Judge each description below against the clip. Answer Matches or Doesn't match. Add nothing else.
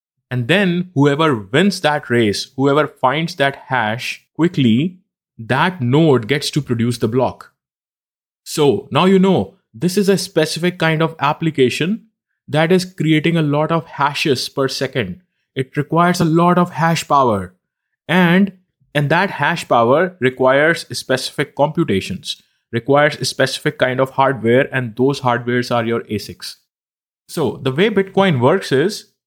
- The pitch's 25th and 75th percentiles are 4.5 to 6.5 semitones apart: Matches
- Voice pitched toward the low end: Doesn't match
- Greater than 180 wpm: Doesn't match